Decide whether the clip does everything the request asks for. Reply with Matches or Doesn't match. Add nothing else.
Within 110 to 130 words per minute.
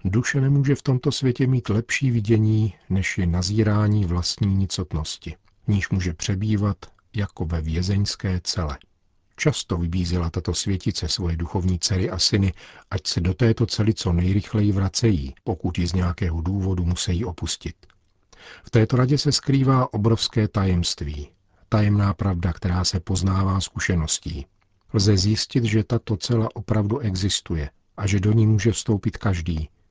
Doesn't match